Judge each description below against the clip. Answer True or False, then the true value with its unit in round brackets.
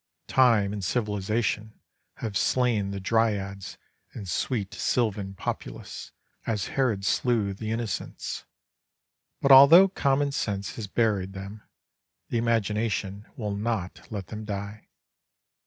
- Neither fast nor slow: False (115 wpm)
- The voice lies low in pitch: True (105 Hz)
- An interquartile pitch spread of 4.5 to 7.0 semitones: False (2.8 semitones)